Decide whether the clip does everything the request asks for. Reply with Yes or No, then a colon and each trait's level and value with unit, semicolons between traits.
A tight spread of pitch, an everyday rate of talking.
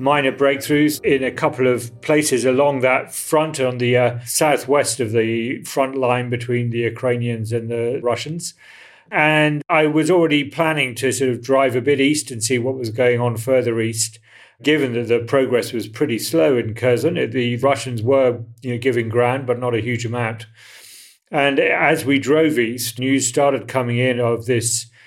No: average, 3.2 semitones; average, 180 wpm